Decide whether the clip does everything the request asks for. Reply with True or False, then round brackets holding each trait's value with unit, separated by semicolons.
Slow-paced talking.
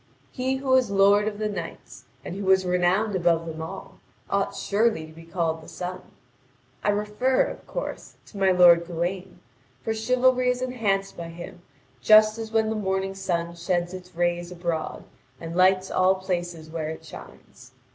False (175 wpm)